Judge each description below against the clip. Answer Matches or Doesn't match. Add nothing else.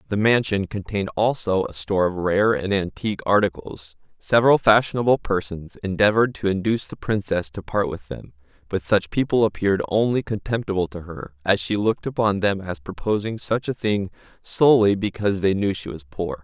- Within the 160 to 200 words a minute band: Matches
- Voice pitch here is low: Matches